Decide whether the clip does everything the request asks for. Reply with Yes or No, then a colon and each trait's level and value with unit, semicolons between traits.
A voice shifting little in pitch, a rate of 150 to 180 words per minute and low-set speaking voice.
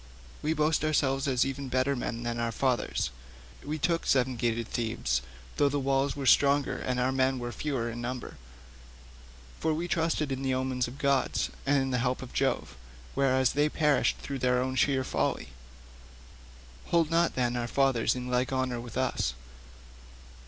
Yes: narrow, 2.3 semitones; average, 175 wpm; low, 130 Hz